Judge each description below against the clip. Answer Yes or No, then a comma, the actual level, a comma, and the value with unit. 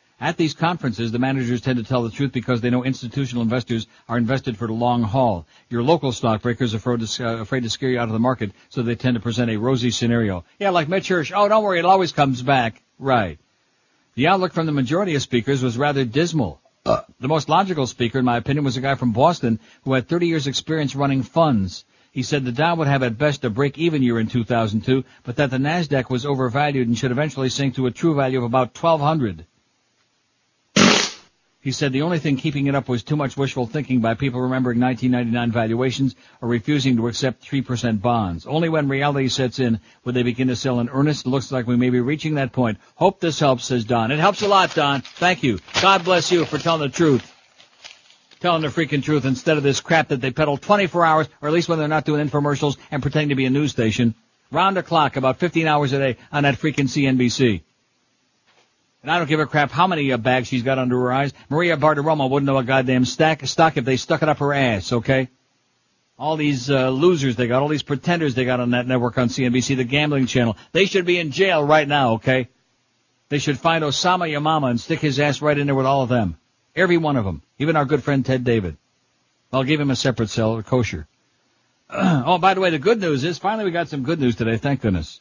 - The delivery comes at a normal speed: No, fast, 225 wpm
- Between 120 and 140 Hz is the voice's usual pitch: Yes, low, 135 Hz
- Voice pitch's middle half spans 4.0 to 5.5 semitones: No, average, 3.6 semitones